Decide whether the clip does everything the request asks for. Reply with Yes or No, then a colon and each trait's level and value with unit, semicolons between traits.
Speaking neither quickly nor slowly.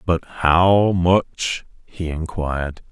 No: slow, 105 wpm